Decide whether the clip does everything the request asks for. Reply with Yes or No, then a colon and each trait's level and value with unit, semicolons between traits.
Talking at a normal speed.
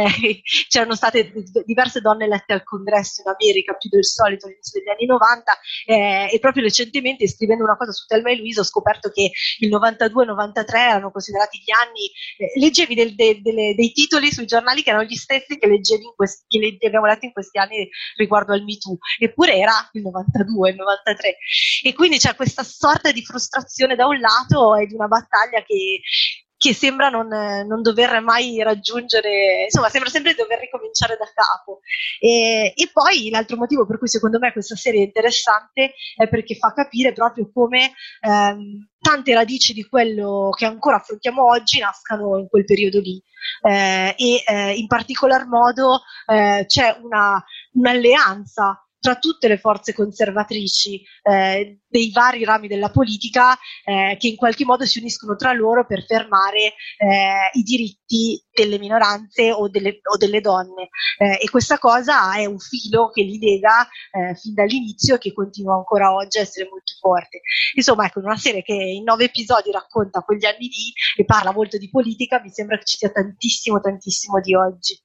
No: fast, 180 wpm